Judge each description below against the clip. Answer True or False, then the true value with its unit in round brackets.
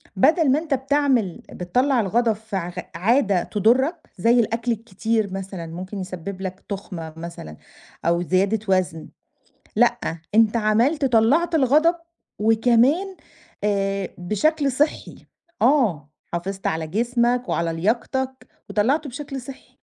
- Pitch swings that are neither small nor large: False (5.9 semitones)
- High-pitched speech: True (225 Hz)